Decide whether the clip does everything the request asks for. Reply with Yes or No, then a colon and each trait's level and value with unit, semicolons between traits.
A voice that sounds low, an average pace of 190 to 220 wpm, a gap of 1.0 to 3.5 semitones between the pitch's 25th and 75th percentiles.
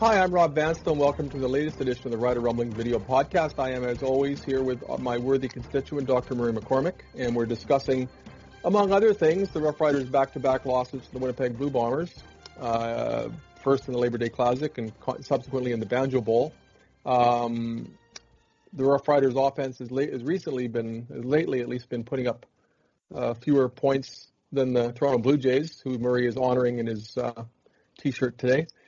Yes: low, 130 Hz; average, 195 wpm; narrow, 2.4 semitones